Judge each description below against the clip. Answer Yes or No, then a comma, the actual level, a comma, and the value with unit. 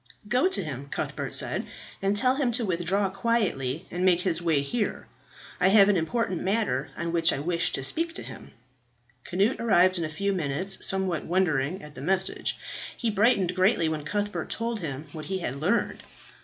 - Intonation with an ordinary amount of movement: Yes, average, 4.4 semitones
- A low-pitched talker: No, medium, 185 Hz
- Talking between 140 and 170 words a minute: No, average, 185 wpm